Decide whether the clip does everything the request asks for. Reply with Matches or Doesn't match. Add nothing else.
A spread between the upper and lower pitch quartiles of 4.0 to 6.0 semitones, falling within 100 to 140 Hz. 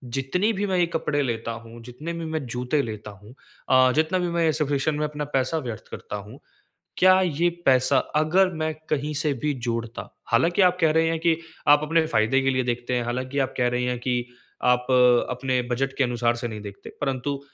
Matches